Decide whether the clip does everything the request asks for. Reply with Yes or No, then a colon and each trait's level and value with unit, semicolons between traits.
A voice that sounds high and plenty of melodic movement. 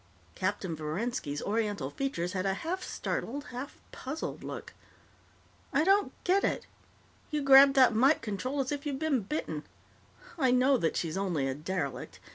Yes: high, 245 Hz; wide, 7.2 semitones